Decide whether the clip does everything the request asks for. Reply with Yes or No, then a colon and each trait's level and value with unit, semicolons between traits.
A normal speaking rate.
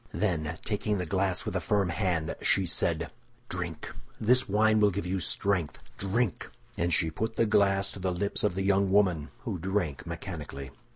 Yes: average, 180 wpm